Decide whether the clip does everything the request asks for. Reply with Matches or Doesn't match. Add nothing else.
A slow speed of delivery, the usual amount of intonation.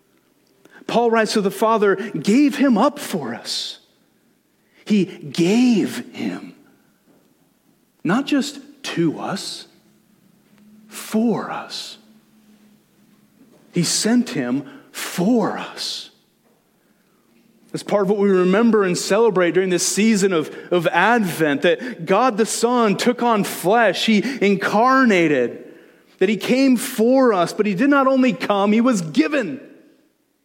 Matches